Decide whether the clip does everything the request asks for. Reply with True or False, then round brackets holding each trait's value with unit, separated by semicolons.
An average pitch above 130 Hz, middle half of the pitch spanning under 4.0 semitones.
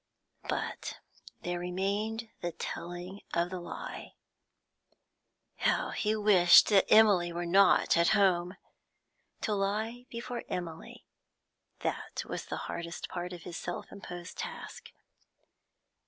True (185 Hz; 3.2 semitones)